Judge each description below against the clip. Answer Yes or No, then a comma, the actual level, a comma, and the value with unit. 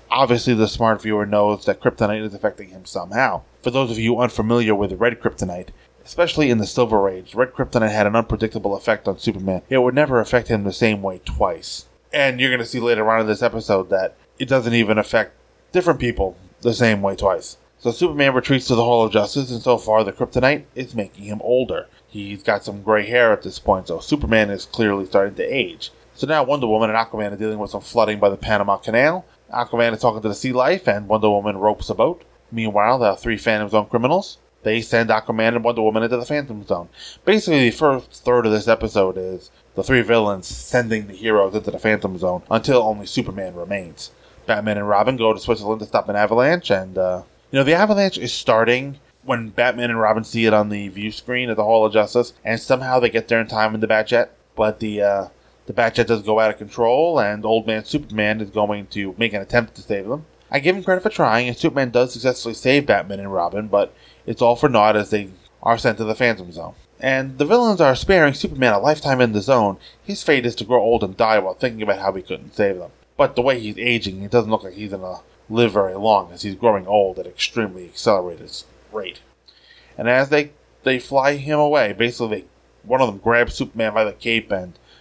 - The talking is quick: Yes, fast, 225 wpm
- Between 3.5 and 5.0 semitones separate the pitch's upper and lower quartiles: No, average, 3.0 semitones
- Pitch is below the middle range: Yes, low, 110 Hz